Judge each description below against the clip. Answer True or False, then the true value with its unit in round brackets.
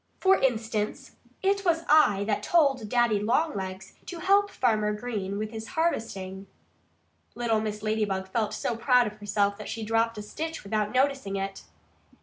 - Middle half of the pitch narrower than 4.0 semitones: False (4.3 semitones)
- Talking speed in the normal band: True (155 wpm)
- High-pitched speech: True (220 Hz)